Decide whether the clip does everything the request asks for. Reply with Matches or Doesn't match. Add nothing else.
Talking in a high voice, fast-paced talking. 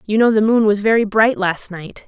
Matches